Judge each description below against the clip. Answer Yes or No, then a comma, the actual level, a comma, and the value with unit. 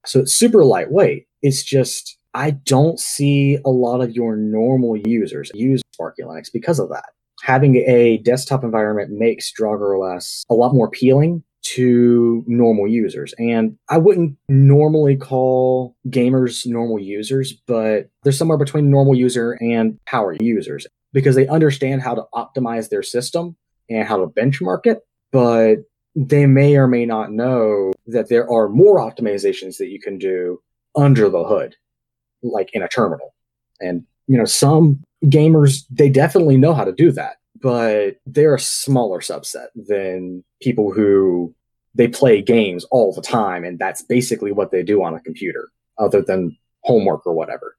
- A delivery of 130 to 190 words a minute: Yes, average, 160 wpm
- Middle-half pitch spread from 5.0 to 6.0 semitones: No, average, 3.7 semitones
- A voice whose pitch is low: Yes, low, 125 Hz